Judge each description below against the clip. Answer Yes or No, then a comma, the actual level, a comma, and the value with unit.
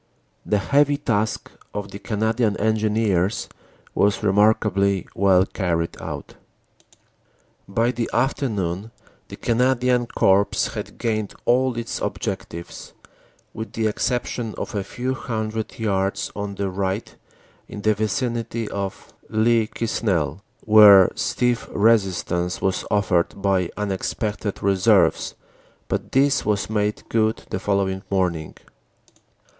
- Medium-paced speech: No, slow, 115 wpm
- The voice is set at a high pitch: No, low, 105 Hz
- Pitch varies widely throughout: No, average, 2.7 semitones